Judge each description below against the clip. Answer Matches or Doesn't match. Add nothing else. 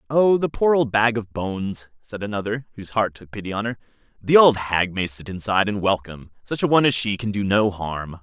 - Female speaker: Doesn't match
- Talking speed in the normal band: Doesn't match